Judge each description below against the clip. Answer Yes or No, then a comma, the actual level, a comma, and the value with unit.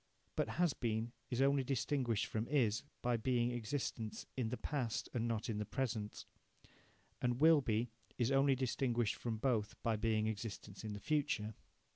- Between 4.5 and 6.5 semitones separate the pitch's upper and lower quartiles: No, average, 3.3 semitones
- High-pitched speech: No, low, 120 Hz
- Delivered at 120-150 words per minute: No, average, 165 wpm